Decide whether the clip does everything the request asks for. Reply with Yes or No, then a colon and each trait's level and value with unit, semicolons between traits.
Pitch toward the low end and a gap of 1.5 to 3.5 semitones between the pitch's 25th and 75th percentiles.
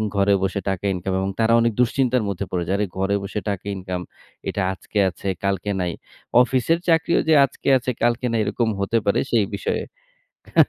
No: low, 100 Hz; average, 4.1 semitones